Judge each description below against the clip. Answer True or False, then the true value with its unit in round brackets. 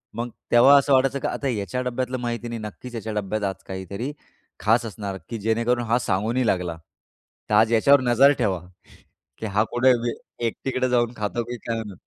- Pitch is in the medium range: False (115 Hz)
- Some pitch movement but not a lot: True (3.0 semitones)